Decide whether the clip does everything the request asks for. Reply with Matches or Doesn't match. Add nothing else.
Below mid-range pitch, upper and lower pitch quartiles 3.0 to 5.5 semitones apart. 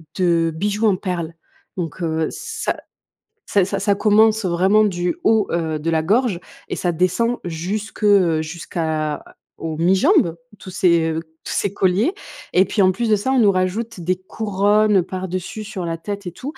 Doesn't match